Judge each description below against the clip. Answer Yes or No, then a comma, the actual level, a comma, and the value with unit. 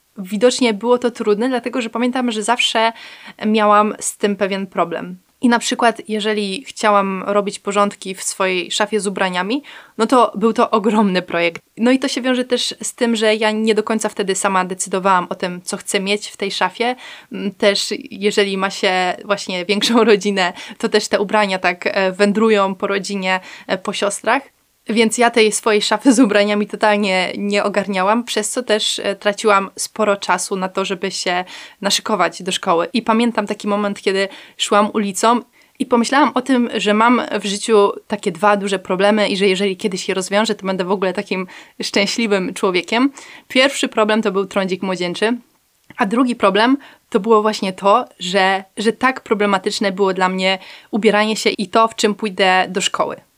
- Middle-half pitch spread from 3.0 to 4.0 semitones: No, narrow, 2.6 semitones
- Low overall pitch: No, high, 210 Hz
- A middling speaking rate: No, fast, 175 wpm